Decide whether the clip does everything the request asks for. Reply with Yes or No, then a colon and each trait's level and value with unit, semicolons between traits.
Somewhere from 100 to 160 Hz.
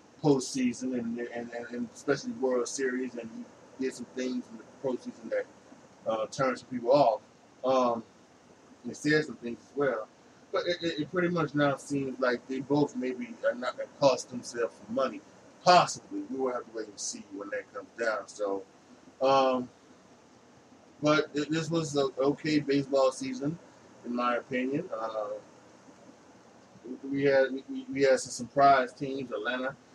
Yes: low, 135 Hz